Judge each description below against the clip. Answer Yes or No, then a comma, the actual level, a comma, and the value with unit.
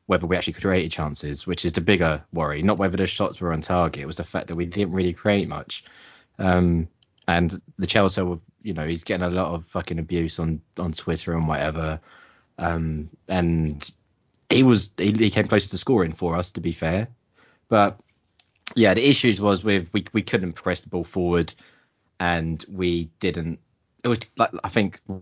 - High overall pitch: No, very low, 90 Hz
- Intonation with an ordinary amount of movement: Yes, average, 3.0 semitones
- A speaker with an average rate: Yes, average, 195 wpm